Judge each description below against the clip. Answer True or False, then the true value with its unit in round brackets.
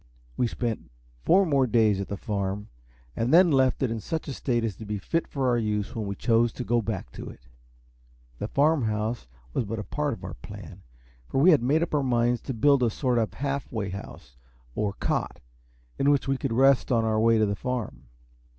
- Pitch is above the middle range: False (120 Hz)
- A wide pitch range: False (4.2 semitones)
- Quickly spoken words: True (225 wpm)